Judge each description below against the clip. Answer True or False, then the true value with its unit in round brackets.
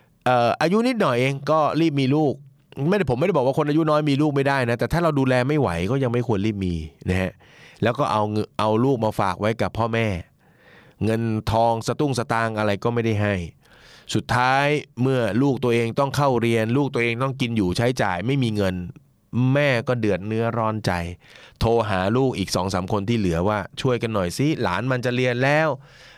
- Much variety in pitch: False (4.2 semitones)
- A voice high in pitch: False (120 Hz)